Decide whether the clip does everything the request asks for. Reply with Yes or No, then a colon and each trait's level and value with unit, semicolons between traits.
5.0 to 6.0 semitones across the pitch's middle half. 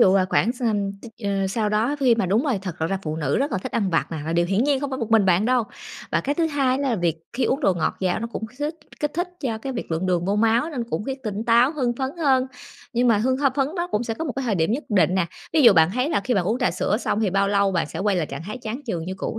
Yes: wide, 5.4 semitones